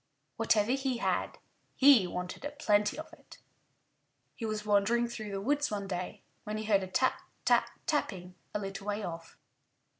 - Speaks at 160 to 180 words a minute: Yes, average, 170 wpm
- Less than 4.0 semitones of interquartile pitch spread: Yes, average, 3.6 semitones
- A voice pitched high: Yes, high, 210 Hz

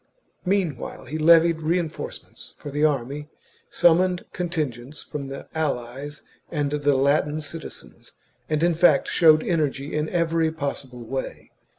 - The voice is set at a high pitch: No, medium, 155 Hz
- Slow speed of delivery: Yes, slow, 125 wpm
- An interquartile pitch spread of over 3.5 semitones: No, average, 2.8 semitones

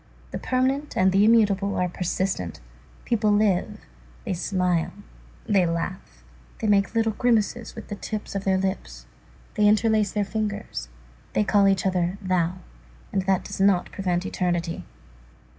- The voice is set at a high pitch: Yes, high, 195 Hz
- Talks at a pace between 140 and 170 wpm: Yes, average, 145 wpm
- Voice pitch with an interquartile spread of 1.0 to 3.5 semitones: Yes, narrow, 2.6 semitones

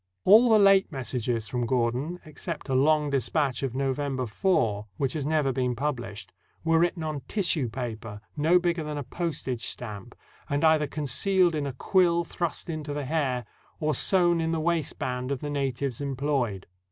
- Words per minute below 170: No, average, 175 wpm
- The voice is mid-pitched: Yes, medium, 145 Hz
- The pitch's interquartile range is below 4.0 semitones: No, average, 4.5 semitones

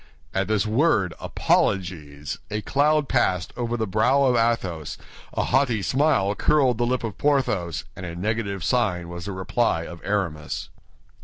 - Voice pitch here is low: Yes, low, 105 Hz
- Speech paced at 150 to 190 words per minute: Yes, average, 155 wpm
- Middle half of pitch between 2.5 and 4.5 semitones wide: No, wide, 5.5 semitones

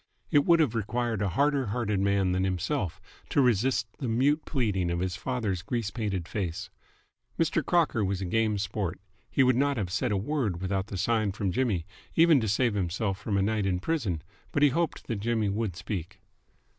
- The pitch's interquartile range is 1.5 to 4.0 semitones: No, average, 5.0 semitones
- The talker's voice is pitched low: Yes, low, 105 Hz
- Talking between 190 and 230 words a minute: Yes, average, 195 wpm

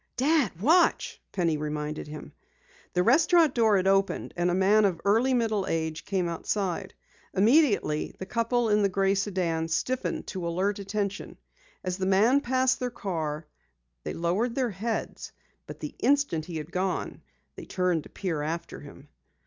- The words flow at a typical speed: Yes, average, 165 wpm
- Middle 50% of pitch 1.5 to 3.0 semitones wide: No, wide, 5.4 semitones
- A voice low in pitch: No, high, 195 Hz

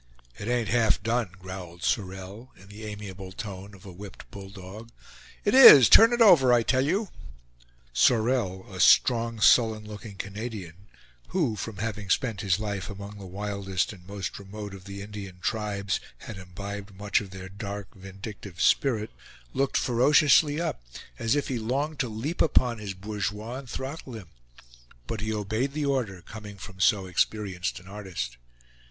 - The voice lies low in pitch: Yes, low, 105 Hz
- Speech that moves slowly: No, average, 165 wpm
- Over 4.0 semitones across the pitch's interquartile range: No, average, 3.5 semitones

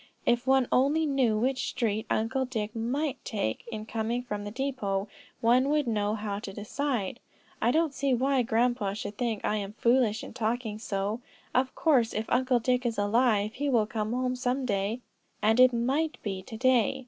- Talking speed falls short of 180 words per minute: No, average, 185 wpm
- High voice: Yes, high, 235 Hz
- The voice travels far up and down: No, average, 3.2 semitones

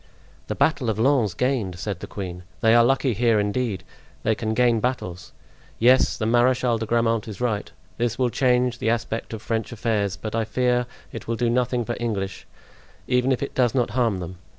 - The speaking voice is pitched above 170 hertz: No, low, 115 Hz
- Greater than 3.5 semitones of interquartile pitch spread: No, narrow, 2.5 semitones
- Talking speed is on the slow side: No, average, 200 wpm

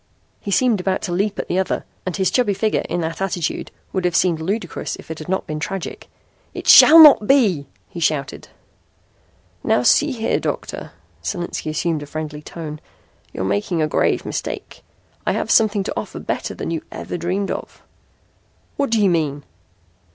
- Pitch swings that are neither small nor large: Yes, average, 4.5 semitones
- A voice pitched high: No, medium, 180 Hz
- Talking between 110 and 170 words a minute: No, average, 180 wpm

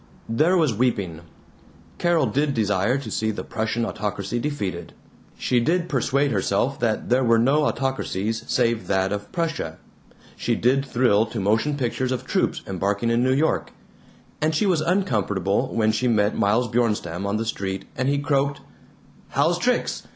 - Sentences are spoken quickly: No, average, 160 wpm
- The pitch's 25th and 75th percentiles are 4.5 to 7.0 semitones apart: Yes, average, 5.2 semitones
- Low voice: Yes, low, 120 Hz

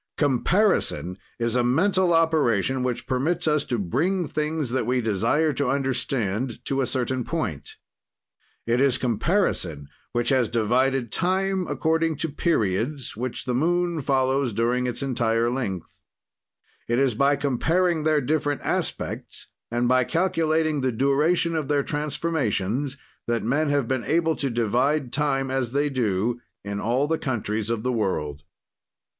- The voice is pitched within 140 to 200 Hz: No, low, 130 Hz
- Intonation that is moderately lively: Yes, average, 4.5 semitones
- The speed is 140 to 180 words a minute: Yes, average, 145 wpm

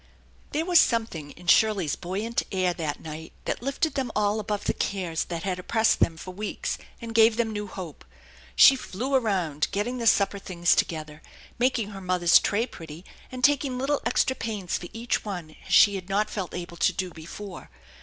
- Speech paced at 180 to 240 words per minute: Yes, average, 190 wpm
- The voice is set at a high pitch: Yes, high, 200 Hz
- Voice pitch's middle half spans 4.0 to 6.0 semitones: Yes, average, 4.9 semitones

